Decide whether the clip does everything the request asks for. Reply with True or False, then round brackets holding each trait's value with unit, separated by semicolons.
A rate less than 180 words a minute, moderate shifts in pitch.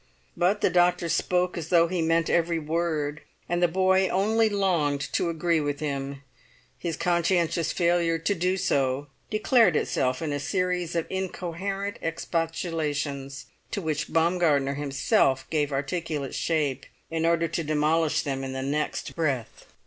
True (150 wpm; 3.4 semitones)